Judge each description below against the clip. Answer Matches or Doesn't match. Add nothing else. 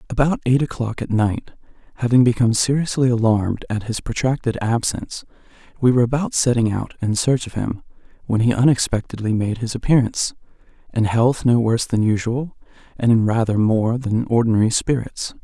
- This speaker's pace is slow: Doesn't match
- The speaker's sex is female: Doesn't match